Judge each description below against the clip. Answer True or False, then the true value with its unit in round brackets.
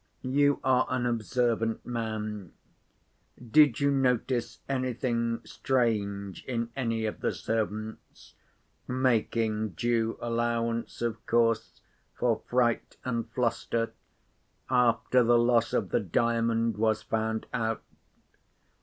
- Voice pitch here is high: False (115 Hz)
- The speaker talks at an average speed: False (100 wpm)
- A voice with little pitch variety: True (1.8 semitones)